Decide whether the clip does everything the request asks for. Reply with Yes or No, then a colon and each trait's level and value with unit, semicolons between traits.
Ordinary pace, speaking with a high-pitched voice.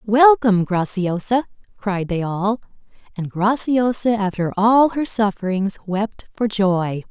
No: slow, 120 wpm; high, 205 Hz